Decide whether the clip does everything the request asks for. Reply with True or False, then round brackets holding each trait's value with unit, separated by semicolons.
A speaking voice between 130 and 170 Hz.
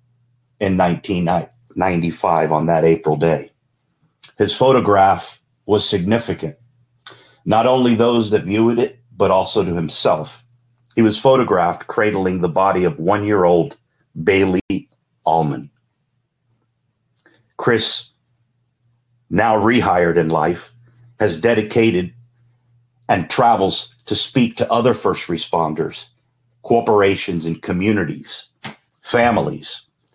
False (115 Hz)